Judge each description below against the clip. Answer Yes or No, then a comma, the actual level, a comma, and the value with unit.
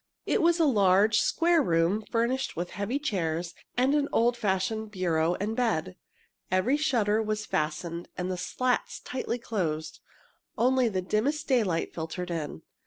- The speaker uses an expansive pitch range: Yes, wide, 6.0 semitones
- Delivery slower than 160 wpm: Yes, average, 150 wpm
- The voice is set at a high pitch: Yes, high, 210 Hz